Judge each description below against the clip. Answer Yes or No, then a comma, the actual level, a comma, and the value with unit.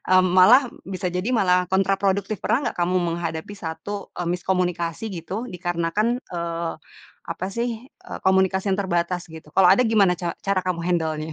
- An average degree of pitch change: No, narrow, 2.1 semitones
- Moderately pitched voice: Yes, medium, 180 Hz